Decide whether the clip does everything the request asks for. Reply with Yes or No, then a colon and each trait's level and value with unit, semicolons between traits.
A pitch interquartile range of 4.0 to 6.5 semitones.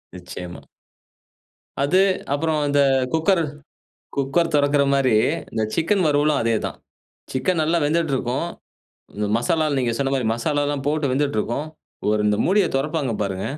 Yes: average, 4.4 semitones